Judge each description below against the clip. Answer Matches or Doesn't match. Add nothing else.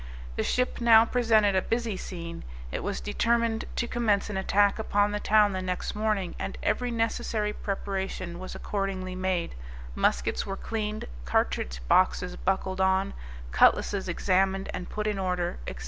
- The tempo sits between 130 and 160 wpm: Matches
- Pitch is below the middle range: Doesn't match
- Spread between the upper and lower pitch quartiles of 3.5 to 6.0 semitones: Doesn't match